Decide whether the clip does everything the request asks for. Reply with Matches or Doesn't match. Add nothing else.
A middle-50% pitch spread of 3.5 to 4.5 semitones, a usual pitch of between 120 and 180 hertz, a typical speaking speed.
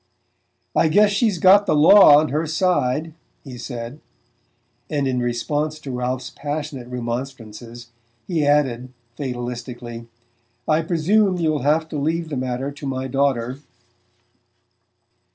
Doesn't match